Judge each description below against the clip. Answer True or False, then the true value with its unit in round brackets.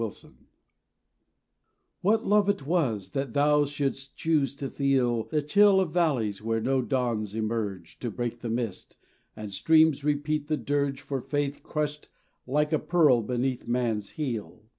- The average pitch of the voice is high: False (135 Hz)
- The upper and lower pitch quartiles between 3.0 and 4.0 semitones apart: False (4.6 semitones)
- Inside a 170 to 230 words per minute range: False (155 wpm)